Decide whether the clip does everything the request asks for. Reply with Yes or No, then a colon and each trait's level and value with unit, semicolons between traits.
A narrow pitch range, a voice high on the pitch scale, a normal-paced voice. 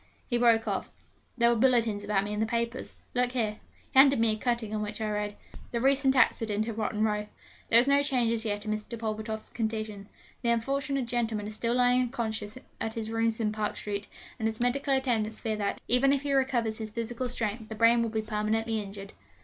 No: narrow, 2.2 semitones; high, 225 Hz; fast, 215 wpm